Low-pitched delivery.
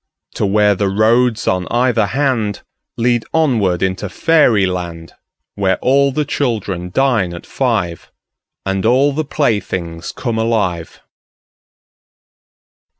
Yes: low, 110 Hz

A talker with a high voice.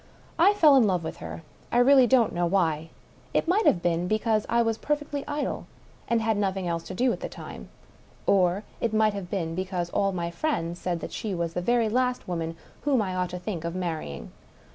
Yes: high, 195 Hz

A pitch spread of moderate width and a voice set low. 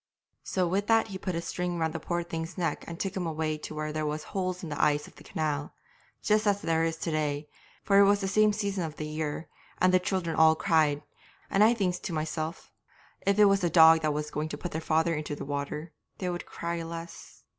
No: average, 3.2 semitones; medium, 165 Hz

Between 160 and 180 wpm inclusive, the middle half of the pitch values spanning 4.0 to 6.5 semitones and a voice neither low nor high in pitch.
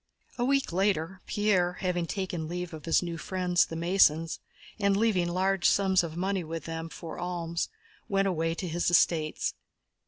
No: average, 165 wpm; narrow, 2.5 semitones; medium, 175 Hz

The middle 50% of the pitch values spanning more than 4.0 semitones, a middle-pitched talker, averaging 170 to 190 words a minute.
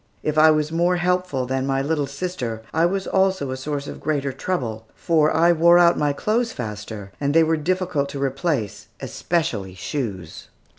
Yes: average, 4.8 semitones; medium, 150 Hz; average, 180 wpm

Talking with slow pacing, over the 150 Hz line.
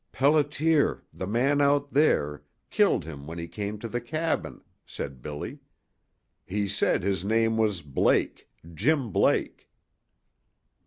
No: slow, 125 wpm; low, 110 Hz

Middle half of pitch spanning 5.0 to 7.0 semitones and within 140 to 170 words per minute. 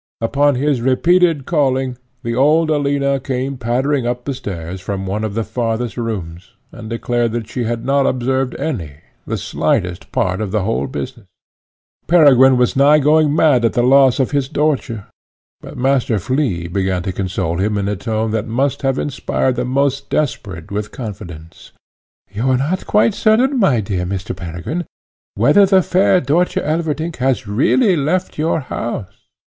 Yes: average, 5.3 semitones; average, 165 wpm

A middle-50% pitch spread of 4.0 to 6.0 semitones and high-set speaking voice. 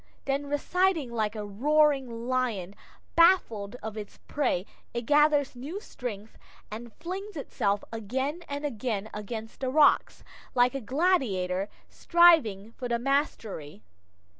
Yes: wide, 5.6 semitones; very high, 250 Hz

